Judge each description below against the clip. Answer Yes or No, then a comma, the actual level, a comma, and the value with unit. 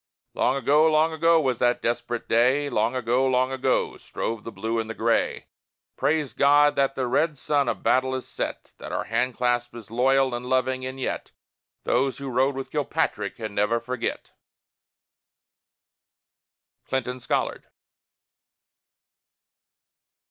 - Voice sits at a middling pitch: No, low, 130 Hz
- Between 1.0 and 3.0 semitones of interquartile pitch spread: Yes, narrow, 2.5 semitones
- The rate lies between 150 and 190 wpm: No, average, 140 wpm